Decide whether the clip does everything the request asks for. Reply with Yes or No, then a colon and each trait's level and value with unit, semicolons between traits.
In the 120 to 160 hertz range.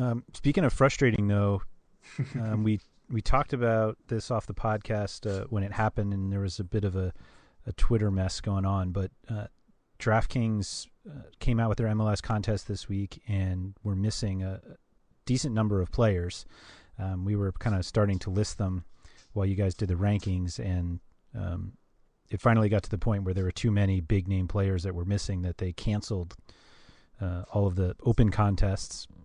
No: low, 100 Hz